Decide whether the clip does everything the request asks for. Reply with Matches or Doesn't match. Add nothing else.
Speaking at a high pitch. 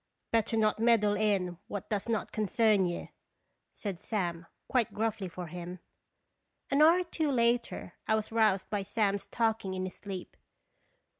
Matches